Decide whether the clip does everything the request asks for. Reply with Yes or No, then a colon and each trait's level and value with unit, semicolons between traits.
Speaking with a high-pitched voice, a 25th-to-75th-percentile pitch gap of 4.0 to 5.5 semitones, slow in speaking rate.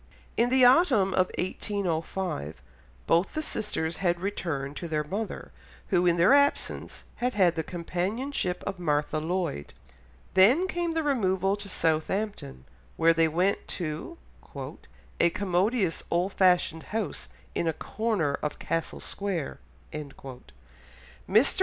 No: medium, 180 Hz; average, 4.4 semitones; slow, 130 wpm